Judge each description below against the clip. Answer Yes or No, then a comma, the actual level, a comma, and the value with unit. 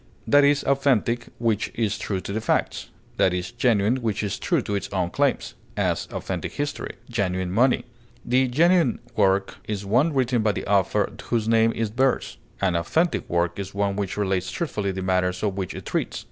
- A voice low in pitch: Yes, low, 105 Hz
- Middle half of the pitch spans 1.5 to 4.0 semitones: No, average, 4.4 semitones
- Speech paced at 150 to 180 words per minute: No, average, 190 wpm